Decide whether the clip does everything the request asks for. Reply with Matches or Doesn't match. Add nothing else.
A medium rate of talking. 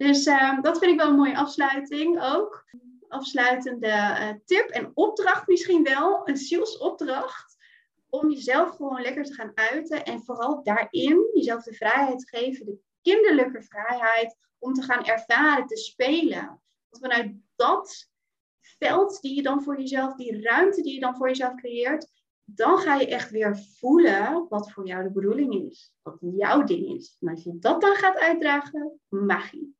Matches